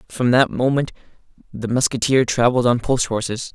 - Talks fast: No, average, 150 wpm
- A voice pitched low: Yes, low, 125 Hz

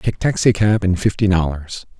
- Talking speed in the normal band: Yes, average, 150 wpm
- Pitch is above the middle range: No, very low, 95 Hz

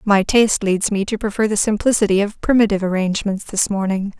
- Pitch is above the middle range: Yes, high, 205 Hz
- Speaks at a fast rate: No, average, 185 wpm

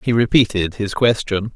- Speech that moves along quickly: No, average, 155 wpm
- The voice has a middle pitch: No, low, 110 Hz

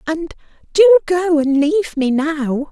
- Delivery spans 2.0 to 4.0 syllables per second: Yes, 3.8 syllables/s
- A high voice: Yes, very high, 320 Hz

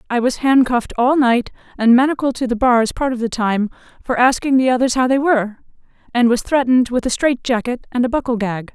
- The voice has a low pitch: No, high, 245 Hz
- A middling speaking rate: No, fast, 215 wpm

